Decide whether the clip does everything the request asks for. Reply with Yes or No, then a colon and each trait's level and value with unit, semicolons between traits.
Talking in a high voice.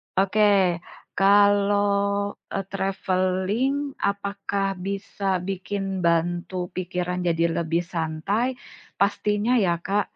Yes: high, 195 Hz